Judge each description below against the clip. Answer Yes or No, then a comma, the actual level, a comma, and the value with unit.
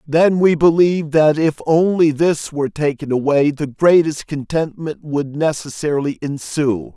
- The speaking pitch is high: No, medium, 150 Hz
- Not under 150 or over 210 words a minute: No, average, 140 wpm